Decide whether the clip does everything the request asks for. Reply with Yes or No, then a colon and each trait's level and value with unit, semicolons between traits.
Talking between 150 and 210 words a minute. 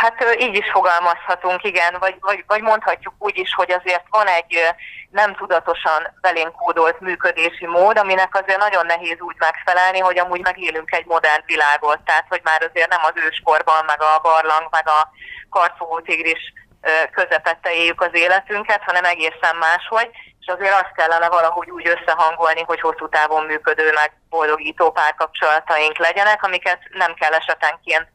Yes: fast, 155 wpm